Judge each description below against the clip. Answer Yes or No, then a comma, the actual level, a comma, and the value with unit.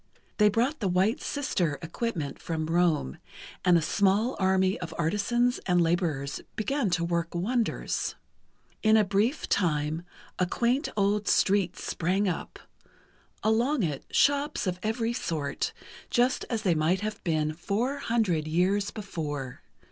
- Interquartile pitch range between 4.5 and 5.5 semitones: Yes, average, 5.2 semitones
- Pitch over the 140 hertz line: Yes, high, 190 Hz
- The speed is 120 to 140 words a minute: Yes, slow, 135 wpm